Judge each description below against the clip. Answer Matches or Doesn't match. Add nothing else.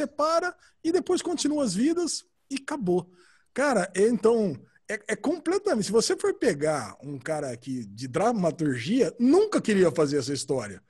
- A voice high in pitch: Matches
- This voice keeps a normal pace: Matches